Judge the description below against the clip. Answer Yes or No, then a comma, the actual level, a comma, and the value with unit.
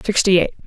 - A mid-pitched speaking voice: No, high, 195 Hz